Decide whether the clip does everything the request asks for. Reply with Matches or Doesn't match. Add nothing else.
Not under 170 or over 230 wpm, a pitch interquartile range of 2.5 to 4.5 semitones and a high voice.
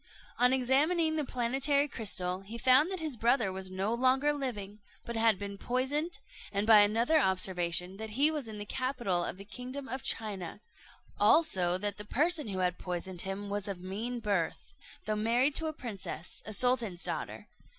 Doesn't match